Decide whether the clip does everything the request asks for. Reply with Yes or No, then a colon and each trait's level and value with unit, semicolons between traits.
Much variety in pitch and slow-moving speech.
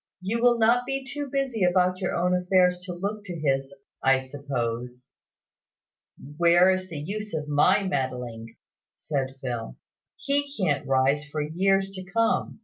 No: wide, 6.5 semitones; average, 150 wpm